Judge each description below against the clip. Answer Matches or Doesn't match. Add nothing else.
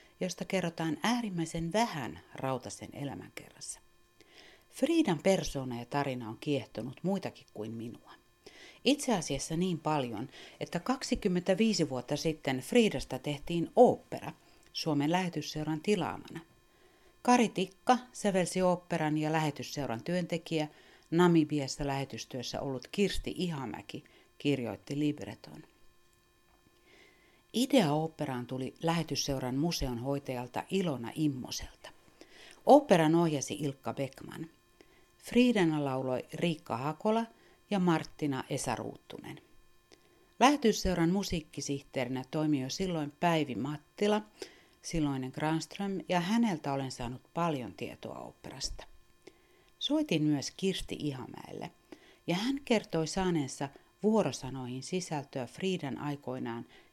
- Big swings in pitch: Matches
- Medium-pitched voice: Matches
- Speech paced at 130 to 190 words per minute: Doesn't match